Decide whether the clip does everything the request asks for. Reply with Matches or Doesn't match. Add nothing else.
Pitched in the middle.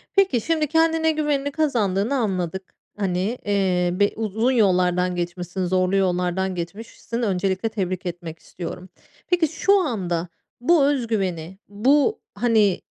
Doesn't match